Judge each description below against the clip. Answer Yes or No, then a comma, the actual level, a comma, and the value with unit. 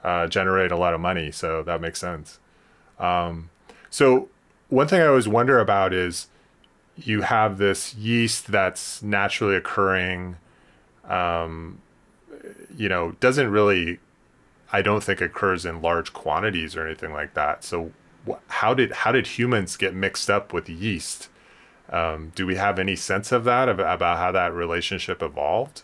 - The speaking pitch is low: Yes, very low, 95 Hz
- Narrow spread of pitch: No, average, 3.5 semitones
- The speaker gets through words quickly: No, average, 160 wpm